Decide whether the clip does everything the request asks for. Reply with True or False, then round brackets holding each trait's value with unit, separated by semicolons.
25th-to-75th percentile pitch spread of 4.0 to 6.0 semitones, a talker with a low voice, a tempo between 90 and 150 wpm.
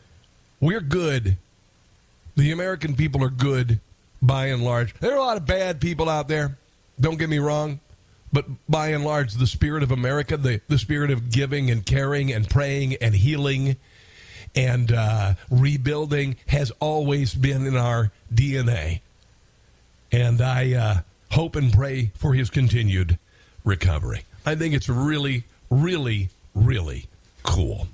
True (5.2 semitones; 130 Hz; 145 wpm)